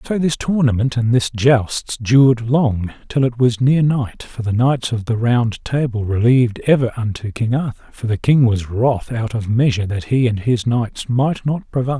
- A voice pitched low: Yes, low, 120 Hz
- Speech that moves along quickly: Yes, fast, 215 wpm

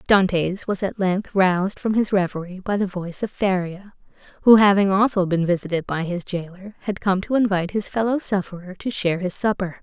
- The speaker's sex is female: Yes, female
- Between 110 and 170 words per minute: No, average, 195 wpm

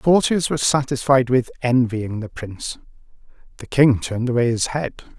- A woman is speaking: No, male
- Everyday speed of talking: Yes, average, 150 wpm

